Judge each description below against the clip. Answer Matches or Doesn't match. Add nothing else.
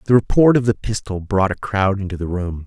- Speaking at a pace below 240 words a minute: Doesn't match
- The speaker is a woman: Doesn't match